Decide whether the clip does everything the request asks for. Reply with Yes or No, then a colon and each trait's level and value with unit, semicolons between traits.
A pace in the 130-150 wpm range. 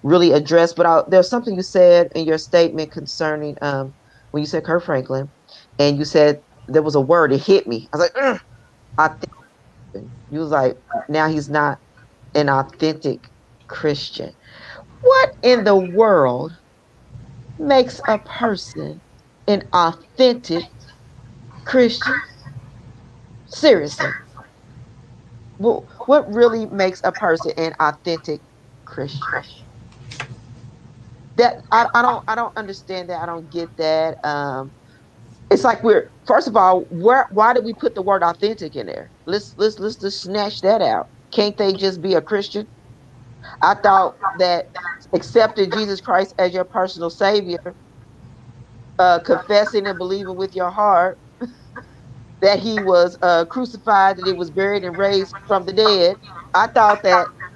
Yes: average, 145 wpm